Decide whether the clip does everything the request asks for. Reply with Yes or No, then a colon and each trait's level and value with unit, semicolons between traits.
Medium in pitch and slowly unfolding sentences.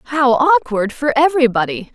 No: very high, 265 Hz; slow, 125 wpm